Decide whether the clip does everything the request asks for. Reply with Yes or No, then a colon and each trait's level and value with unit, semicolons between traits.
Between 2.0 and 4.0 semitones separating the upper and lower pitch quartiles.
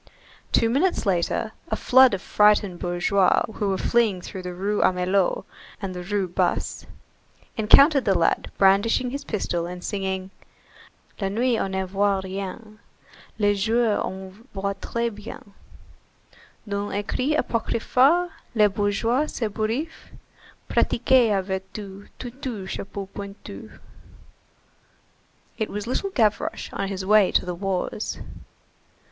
Yes: average, 3.1 semitones